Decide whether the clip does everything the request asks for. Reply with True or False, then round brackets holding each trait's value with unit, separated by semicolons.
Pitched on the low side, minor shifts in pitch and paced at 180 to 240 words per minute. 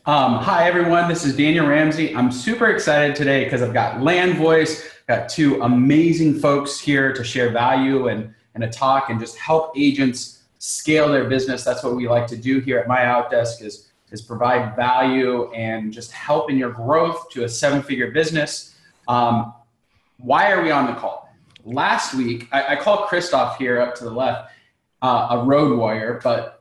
False (130 Hz; 3.7 semitones; 185 wpm)